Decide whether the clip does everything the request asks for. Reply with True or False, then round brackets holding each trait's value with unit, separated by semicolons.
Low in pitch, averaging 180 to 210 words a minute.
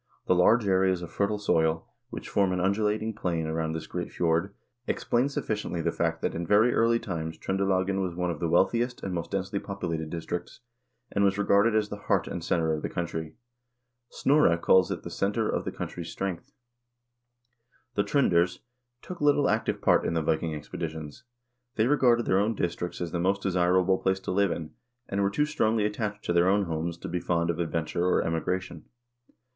True (95 Hz; 195 wpm)